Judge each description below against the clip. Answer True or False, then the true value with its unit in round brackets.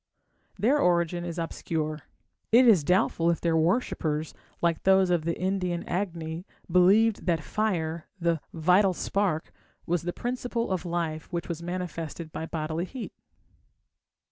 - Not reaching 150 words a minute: True (140 wpm)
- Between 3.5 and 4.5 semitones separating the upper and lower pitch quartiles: False (2.7 semitones)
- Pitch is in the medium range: True (175 Hz)